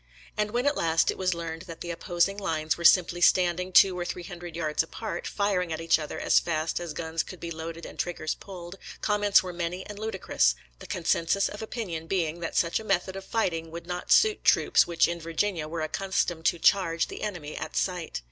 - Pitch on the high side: No, medium, 175 Hz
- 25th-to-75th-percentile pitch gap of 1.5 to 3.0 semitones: Yes, narrow, 2.6 semitones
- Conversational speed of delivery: No, fast, 220 wpm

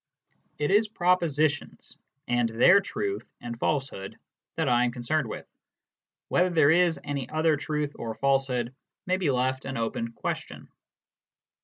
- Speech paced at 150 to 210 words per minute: No, average, 140 wpm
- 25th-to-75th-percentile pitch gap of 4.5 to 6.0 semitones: Yes, average, 5.1 semitones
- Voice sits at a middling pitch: Yes, medium, 145 Hz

